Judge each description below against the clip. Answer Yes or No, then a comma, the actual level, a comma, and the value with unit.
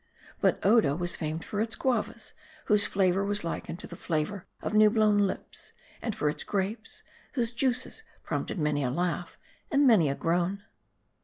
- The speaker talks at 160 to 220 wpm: Yes, average, 170 wpm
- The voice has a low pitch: No, high, 200 Hz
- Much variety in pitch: No, average, 4.4 semitones